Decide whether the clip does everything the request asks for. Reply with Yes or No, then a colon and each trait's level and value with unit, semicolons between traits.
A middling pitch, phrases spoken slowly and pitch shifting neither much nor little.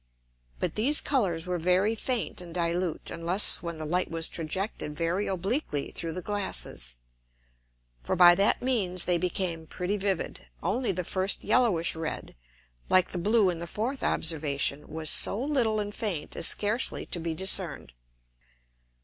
No: medium, 180 Hz; average, 155 wpm; average, 3.9 semitones